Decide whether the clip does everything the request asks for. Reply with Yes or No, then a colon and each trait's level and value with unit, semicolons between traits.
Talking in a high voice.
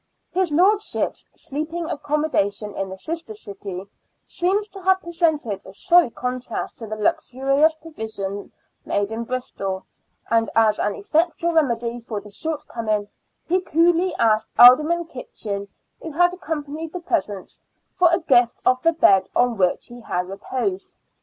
Yes: very high, 260 Hz